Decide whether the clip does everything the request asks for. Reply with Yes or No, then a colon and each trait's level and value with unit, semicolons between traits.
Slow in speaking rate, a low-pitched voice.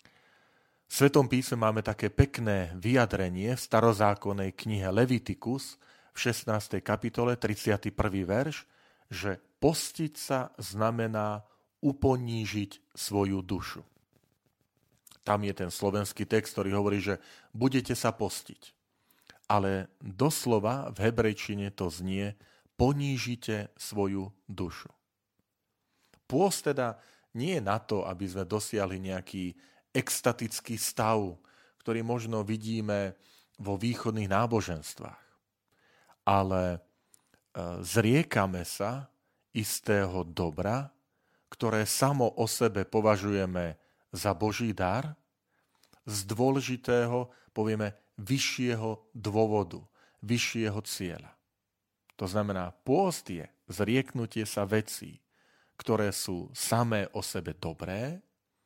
Yes: slow, 95 wpm; low, 110 Hz